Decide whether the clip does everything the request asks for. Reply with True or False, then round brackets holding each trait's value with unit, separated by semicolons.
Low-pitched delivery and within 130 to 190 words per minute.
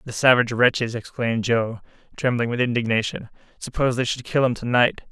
True (120 Hz; 175 wpm)